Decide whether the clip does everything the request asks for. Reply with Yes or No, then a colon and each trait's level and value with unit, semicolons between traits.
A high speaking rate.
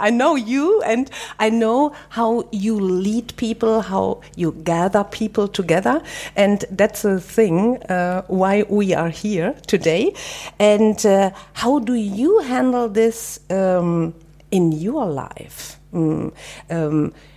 No: average, 130 wpm